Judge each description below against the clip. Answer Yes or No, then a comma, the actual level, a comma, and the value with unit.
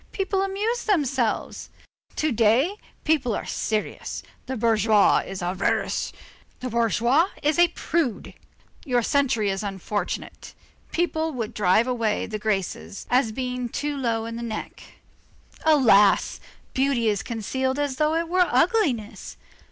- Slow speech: Yes, slow, 130 wpm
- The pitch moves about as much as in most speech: No, wide, 5.8 semitones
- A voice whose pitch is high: Yes, high, 245 Hz